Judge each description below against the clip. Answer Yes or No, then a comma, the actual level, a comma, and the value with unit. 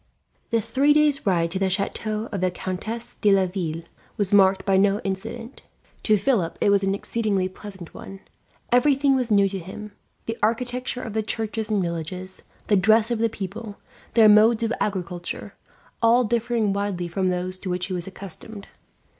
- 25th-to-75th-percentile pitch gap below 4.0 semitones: Yes, average, 3.3 semitones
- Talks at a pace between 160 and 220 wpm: Yes, average, 175 wpm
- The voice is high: Yes, high, 205 Hz